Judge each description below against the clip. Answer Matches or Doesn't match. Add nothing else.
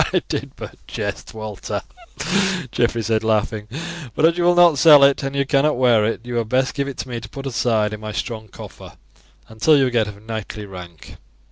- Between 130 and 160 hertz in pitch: Doesn't match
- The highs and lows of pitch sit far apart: Doesn't match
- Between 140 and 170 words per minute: Doesn't match